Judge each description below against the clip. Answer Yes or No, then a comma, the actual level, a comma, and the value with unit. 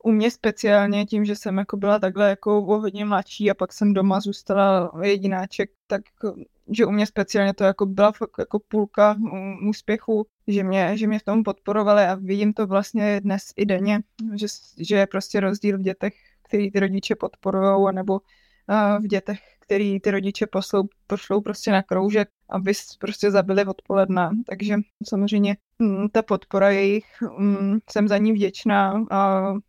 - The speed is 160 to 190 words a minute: Yes, fast, 170 wpm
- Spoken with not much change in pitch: Yes, narrow, 1.2 semitones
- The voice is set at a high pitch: Yes, high, 200 Hz